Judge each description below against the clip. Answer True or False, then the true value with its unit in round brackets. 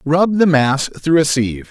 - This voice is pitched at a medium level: True (150 Hz)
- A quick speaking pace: True (210 wpm)